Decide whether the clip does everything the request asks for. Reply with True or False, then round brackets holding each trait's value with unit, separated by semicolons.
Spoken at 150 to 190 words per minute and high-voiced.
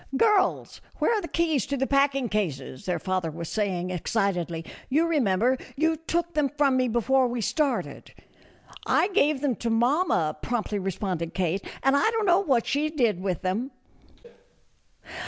True (170 wpm; 245 Hz)